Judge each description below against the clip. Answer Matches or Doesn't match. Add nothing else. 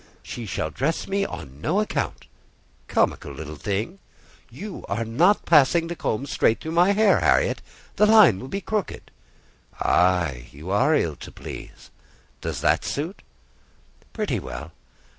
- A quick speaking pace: Doesn't match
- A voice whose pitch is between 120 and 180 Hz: Matches